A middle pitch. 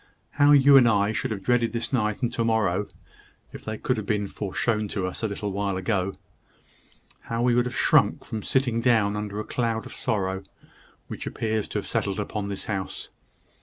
No: low, 110 Hz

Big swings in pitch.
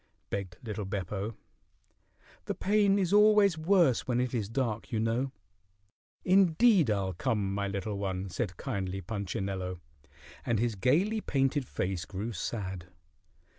Yes: wide, 7.1 semitones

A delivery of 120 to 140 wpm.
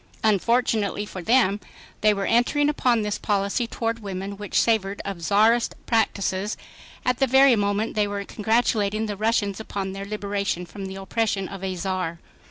No: average, 165 wpm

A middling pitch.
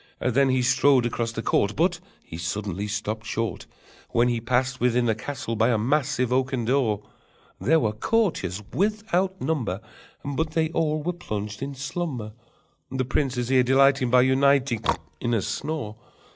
No: low, 130 Hz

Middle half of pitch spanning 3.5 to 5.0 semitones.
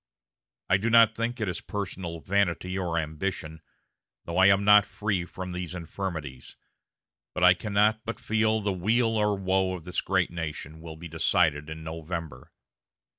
Yes: average, 3.8 semitones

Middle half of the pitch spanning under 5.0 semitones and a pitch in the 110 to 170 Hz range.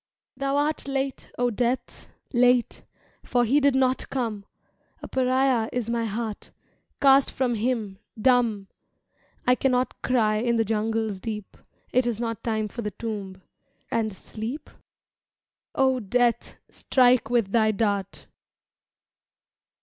No: average, 2.8 semitones; high, 235 Hz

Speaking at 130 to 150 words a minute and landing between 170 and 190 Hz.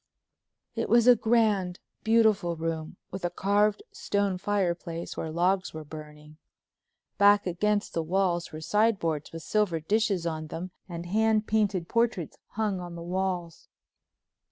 Yes: average, 140 wpm; medium, 185 Hz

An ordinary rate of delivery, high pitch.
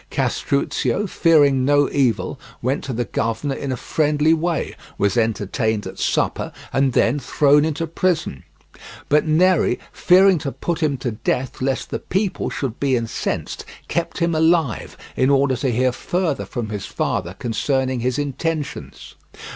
No: average, 150 wpm; medium, 140 Hz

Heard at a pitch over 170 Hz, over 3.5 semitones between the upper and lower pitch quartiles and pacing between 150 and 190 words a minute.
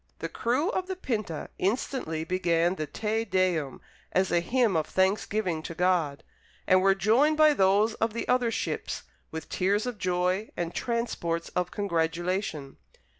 Yes: high, 190 Hz; average, 4.8 semitones; average, 155 wpm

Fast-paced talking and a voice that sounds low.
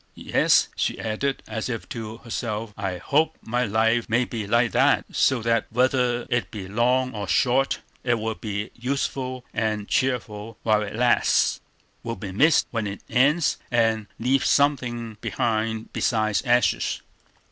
No: average, 150 wpm; low, 115 Hz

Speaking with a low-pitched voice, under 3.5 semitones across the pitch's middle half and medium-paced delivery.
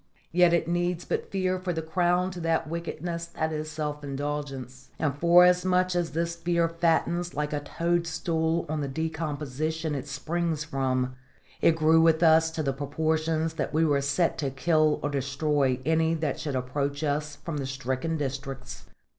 No: medium, 160 Hz; average, 2.7 semitones; average, 170 wpm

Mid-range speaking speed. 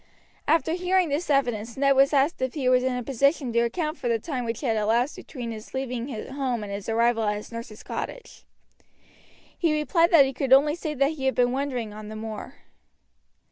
No: fast, 210 wpm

